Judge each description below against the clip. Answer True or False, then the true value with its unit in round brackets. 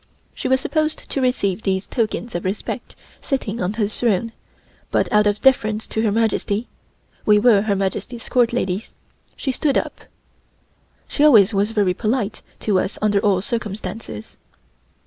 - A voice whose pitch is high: True (215 Hz)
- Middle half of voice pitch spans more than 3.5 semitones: False (3.1 semitones)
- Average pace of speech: True (155 wpm)